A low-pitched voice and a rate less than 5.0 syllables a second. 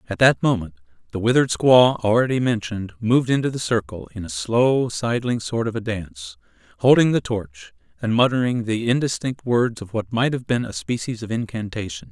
No: low, 110 Hz; 5.4 syllables/s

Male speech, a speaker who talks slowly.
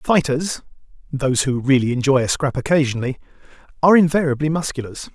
Yes: male; slow, 105 wpm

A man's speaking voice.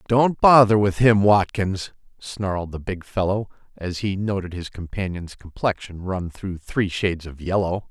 Yes: male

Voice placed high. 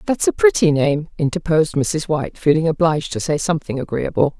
No: medium, 160 Hz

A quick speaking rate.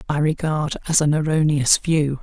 No: average, 160 wpm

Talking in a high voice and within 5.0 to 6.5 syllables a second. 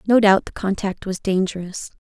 Yes: high, 195 Hz; 5.1 syllables/s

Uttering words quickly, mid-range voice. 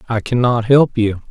No: fast, 230 wpm; low, 120 Hz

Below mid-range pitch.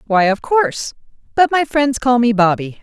No: high, 245 Hz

